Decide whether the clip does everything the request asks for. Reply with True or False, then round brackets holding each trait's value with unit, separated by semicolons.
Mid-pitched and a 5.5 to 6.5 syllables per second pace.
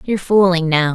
True (175 Hz; 5.9 syllables/s)